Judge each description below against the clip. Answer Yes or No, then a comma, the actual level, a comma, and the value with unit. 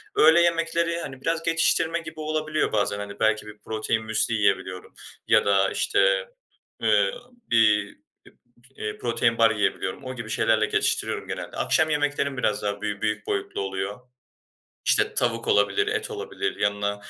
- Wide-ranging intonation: Yes, wide, 7.9 semitones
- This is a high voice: No, low, 115 Hz